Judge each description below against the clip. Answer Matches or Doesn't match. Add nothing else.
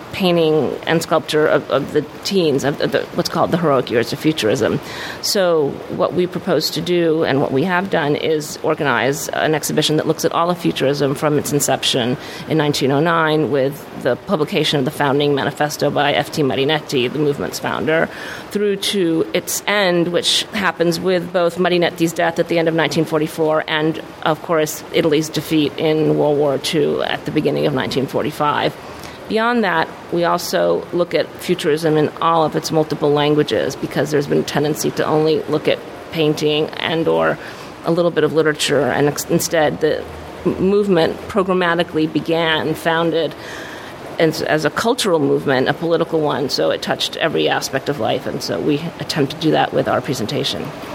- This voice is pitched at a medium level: Matches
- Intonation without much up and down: Matches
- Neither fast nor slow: Matches